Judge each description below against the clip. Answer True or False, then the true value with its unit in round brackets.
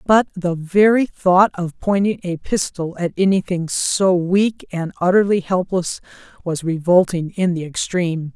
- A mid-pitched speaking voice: True (180 Hz)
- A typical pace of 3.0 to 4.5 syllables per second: True (4.3 syllables/s)